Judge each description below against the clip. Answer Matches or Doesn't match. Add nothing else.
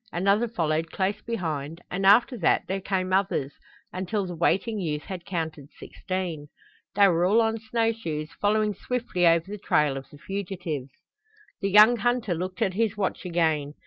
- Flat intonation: Doesn't match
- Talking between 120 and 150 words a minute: Doesn't match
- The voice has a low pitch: Doesn't match